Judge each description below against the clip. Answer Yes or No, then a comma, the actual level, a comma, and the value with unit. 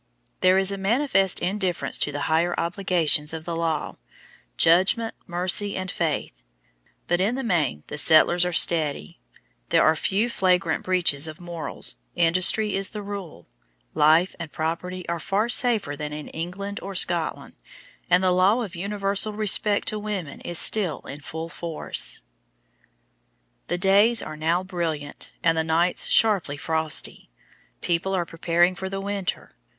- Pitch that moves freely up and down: No, average, 3.4 semitones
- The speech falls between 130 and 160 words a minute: Yes, average, 150 wpm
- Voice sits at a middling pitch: Yes, medium, 180 Hz